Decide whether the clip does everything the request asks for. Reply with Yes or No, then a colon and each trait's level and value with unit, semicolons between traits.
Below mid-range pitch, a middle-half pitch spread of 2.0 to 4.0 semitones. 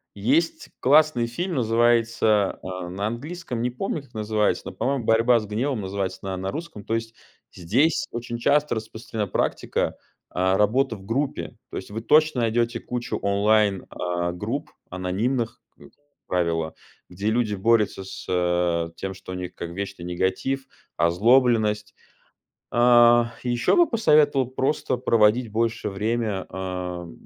No: low, 110 Hz; average, 4.4 semitones